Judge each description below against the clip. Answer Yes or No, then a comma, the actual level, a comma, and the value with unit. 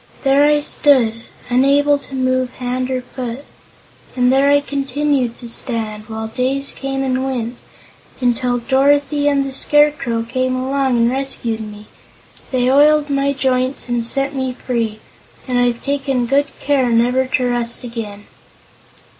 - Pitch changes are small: Yes, narrow, 2.3 semitones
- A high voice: Yes, very high, 255 Hz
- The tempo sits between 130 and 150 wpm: Yes, average, 145 wpm